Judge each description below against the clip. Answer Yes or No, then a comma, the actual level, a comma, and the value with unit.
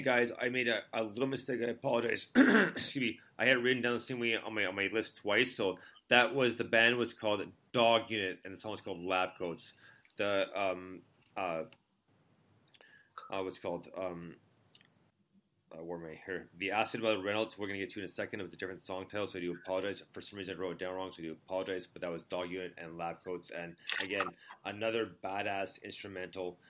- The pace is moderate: No, fast, 220 wpm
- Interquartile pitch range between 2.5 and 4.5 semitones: Yes, average, 4.0 semitones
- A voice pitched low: Yes, low, 100 Hz